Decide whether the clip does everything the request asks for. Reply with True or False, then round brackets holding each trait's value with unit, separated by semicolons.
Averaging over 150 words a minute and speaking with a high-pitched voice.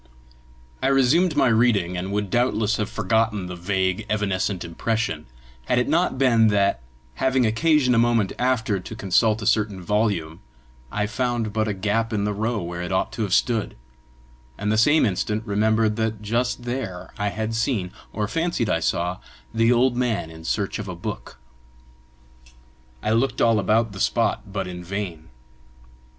False (170 wpm; 110 Hz)